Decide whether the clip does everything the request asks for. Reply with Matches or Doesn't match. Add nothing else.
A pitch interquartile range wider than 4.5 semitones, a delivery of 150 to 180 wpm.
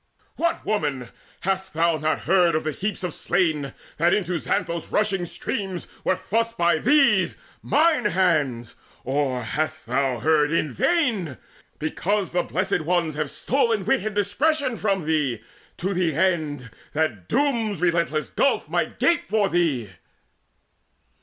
Doesn't match